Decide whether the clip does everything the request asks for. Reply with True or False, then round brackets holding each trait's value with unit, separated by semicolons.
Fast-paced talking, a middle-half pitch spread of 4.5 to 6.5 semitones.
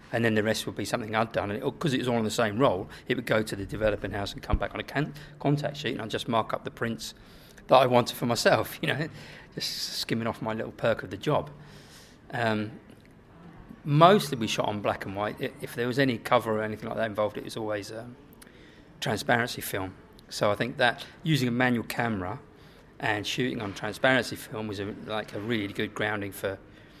False (230 wpm; 3.6 semitones)